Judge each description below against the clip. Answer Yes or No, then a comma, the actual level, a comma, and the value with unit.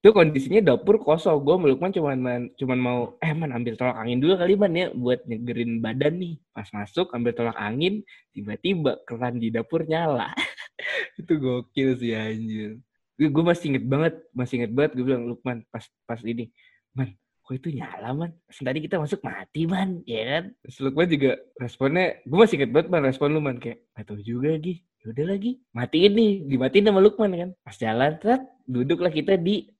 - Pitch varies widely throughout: Yes, wide, 6.3 semitones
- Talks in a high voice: No, medium, 140 Hz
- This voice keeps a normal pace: No, fast, 185 wpm